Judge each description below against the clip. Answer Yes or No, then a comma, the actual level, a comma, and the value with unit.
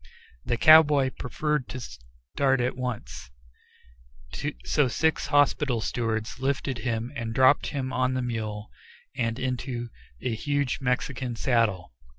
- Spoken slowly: Yes, slow, 125 wpm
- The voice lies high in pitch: No, low, 125 Hz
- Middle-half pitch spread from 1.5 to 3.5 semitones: Yes, average, 2.9 semitones